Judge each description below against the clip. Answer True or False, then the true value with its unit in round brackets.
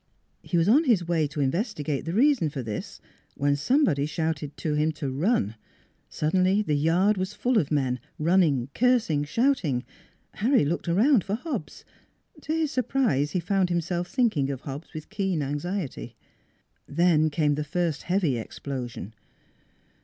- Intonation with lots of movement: True (6.0 semitones)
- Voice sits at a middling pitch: True (165 Hz)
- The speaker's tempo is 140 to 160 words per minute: True (155 wpm)